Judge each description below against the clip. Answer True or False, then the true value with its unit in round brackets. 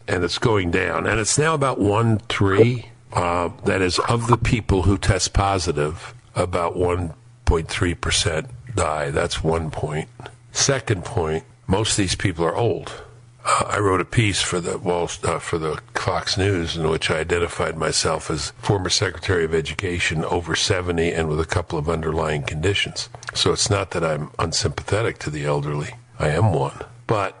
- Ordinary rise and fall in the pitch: False (5.7 semitones)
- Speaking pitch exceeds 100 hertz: False (95 Hz)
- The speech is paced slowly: False (175 wpm)